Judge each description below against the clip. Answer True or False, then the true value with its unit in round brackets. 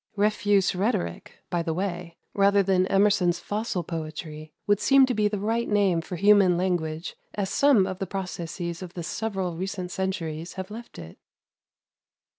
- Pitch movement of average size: True (3.1 semitones)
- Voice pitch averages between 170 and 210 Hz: True (190 Hz)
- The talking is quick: False (160 wpm)